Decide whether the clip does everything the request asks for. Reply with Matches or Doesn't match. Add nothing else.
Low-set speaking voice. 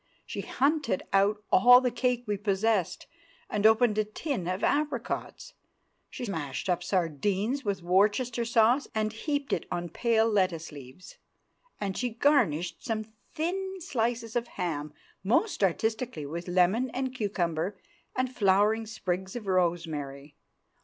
Doesn't match